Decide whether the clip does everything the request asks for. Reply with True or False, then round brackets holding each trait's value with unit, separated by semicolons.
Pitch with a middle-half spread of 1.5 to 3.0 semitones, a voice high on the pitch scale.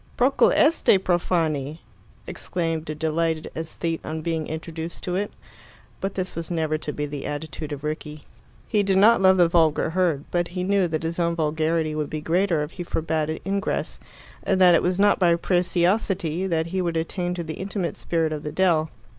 False (2.6 semitones; 165 Hz)